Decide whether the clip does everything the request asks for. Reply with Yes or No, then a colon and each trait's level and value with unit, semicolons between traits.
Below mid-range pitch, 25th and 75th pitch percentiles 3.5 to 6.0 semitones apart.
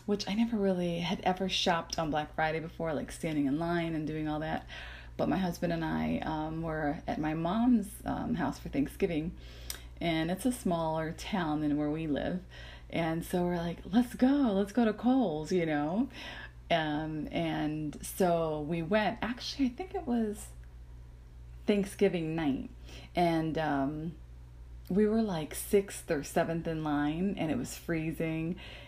No: medium, 165 Hz; average, 4.6 semitones